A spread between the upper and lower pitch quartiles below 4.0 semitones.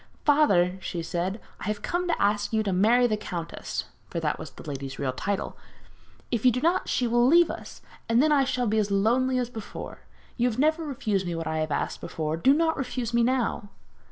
No: wide, 5.5 semitones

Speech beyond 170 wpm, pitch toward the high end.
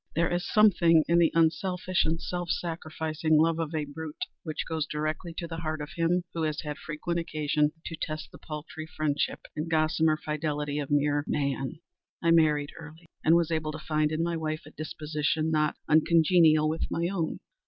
No: average, 185 wpm; medium, 155 Hz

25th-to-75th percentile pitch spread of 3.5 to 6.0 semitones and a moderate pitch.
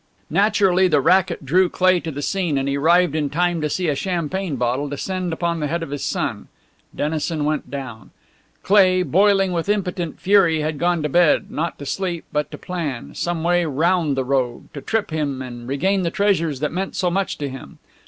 Yes: average, 4.2 semitones; medium, 165 Hz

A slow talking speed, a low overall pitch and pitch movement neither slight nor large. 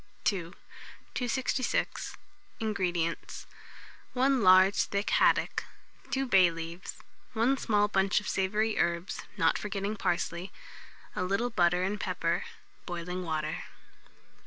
No: slow, 110 wpm; high, 190 Hz; average, 3.5 semitones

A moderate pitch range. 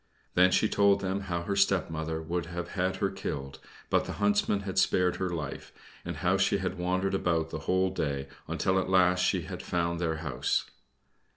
No: narrow, 2.3 semitones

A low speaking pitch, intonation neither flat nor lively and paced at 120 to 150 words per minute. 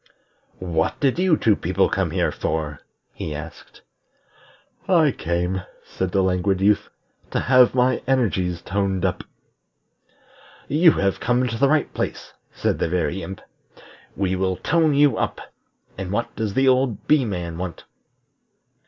No: low, 100 Hz; wide, 6.3 semitones; average, 145 wpm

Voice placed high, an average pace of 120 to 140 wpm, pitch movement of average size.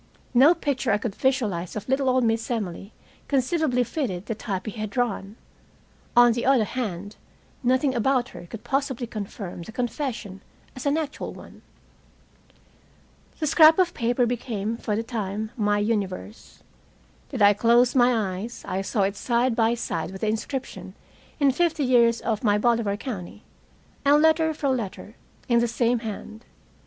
No: high, 235 Hz; average, 160 wpm; average, 3.8 semitones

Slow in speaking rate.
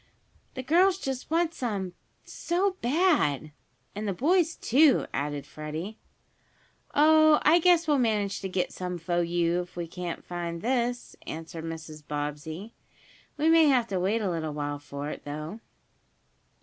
No: average, 150 wpm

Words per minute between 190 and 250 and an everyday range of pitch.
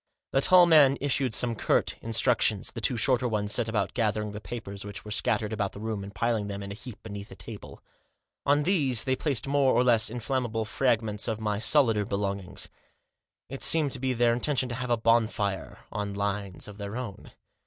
Yes: average, 200 wpm; average, 3.6 semitones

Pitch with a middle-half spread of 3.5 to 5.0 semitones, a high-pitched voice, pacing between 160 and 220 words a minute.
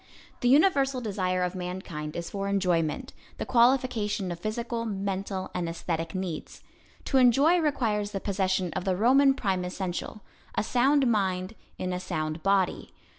No: average, 4.7 semitones; high, 195 Hz; average, 150 wpm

